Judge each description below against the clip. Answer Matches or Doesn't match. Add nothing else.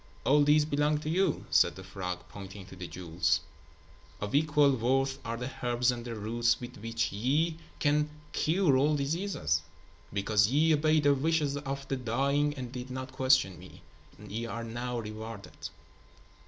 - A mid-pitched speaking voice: Doesn't match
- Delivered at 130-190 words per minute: Matches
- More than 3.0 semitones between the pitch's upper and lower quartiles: Matches